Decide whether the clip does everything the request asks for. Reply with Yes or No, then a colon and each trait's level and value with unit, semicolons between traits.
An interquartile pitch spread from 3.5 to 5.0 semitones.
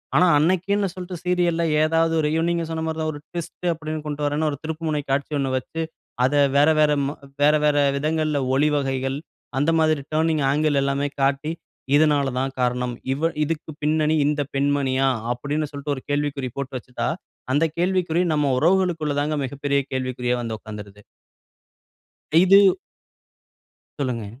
No: average, 2.7 semitones